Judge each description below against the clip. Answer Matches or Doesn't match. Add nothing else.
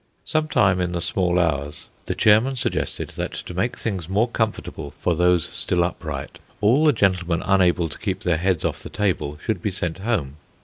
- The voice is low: Matches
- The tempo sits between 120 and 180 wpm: Doesn't match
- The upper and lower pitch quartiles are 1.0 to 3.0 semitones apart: Doesn't match